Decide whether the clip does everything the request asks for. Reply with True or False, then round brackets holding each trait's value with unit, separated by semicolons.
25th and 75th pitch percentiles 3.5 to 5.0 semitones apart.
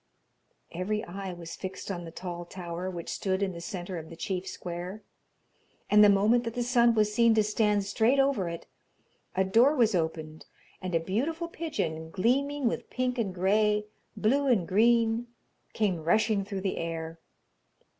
True (4.7 semitones)